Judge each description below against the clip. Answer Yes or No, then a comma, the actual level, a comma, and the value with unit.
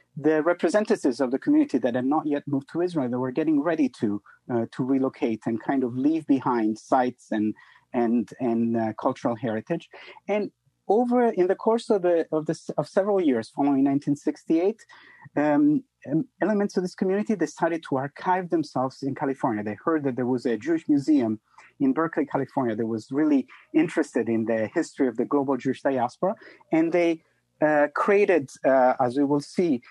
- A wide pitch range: Yes, wide, 7.5 semitones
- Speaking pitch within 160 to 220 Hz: No, medium, 150 Hz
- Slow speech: No, average, 185 wpm